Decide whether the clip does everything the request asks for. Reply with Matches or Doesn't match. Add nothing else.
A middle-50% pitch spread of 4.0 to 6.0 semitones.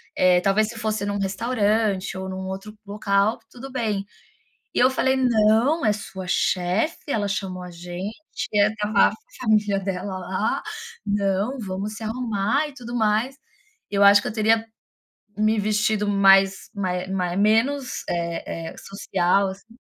Doesn't match